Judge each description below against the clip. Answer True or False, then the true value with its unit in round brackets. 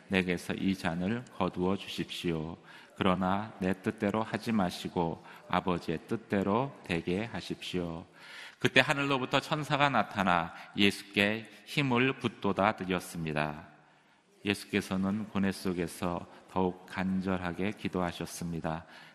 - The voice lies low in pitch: True (95 Hz)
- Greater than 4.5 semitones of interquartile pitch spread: False (3.1 semitones)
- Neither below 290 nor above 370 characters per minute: False (275 characters per minute)